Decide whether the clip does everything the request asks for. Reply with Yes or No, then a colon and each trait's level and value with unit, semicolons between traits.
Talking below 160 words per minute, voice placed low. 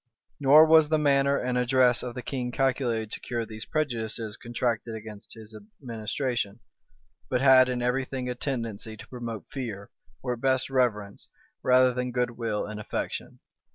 No: average, 165 wpm; low, 125 Hz